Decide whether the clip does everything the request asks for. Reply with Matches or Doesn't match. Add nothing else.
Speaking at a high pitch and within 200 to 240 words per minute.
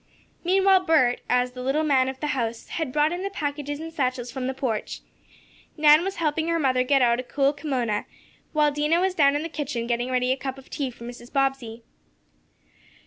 Matches